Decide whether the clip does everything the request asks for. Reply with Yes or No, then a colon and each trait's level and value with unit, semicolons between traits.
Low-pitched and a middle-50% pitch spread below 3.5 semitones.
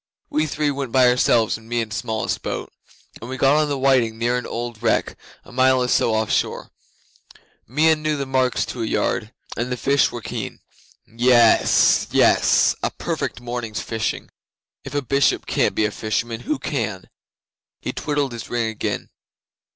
Yes: low, 125 Hz; average, 3.1 semitones